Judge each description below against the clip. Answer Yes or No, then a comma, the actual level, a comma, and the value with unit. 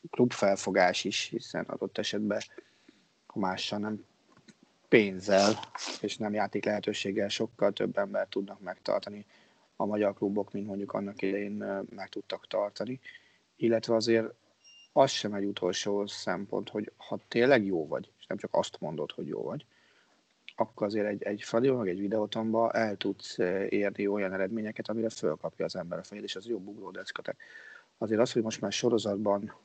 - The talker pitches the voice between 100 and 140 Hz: Yes, low, 105 Hz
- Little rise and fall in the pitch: Yes, narrow, 1.9 semitones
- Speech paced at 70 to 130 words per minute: No, fast, 155 wpm